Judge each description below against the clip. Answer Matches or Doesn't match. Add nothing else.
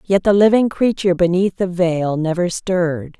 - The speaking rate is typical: Matches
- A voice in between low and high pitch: Matches